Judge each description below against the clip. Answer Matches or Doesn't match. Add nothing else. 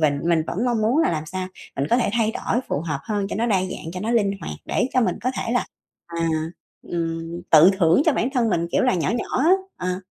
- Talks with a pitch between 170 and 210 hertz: Matches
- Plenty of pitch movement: Matches